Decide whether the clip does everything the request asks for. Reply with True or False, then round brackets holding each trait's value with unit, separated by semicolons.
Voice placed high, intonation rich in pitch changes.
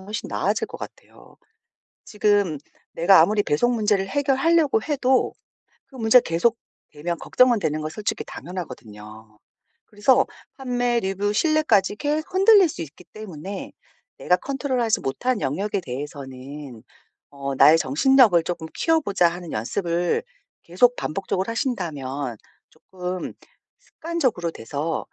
True (195 Hz; 7.9 semitones)